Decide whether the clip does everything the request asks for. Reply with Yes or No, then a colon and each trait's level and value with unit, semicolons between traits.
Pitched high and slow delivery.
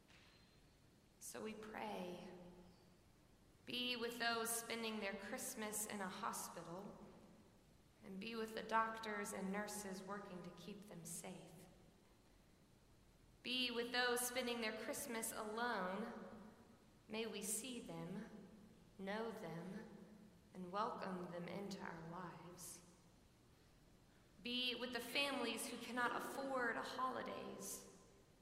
Yes: high, 210 Hz; slow, 110 wpm